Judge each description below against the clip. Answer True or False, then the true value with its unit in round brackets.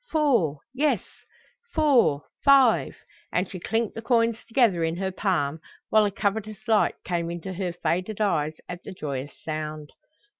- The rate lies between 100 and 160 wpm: True (150 wpm)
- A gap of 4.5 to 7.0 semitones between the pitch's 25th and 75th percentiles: True (5.5 semitones)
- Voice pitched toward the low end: False (190 Hz)